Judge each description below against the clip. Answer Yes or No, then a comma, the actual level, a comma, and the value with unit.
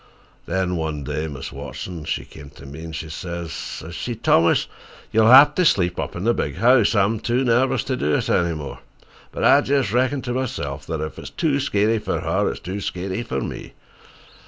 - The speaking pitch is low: Yes, very low, 95 Hz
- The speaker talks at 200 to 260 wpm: Yes, fast, 205 wpm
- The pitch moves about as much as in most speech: No, wide, 7.3 semitones